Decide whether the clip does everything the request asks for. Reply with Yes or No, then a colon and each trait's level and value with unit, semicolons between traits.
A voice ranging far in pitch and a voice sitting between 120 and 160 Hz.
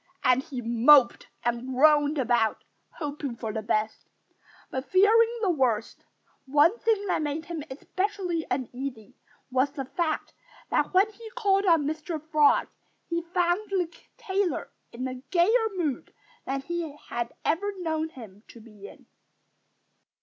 No: wide, 6.0 semitones; very high, 300 Hz